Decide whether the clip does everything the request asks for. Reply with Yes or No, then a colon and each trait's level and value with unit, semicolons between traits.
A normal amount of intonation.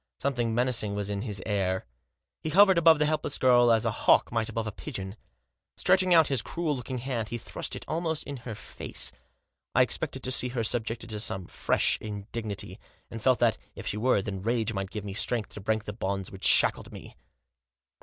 Yes: average, 4.0 semitones